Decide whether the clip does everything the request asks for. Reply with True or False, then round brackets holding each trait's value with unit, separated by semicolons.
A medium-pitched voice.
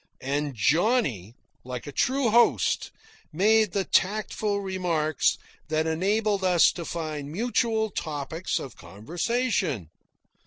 True (175 Hz)